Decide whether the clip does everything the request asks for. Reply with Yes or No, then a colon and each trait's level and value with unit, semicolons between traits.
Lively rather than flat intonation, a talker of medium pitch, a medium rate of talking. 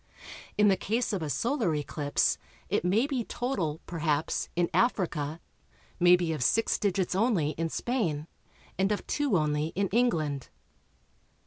Yes: wide, 6.4 semitones; medium, 180 Hz; average, 145 wpm